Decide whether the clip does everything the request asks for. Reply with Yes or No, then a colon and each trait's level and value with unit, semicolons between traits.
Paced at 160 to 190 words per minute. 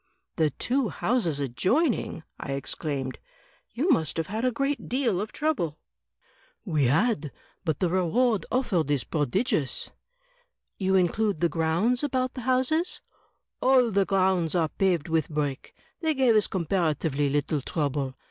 No: average, 145 wpm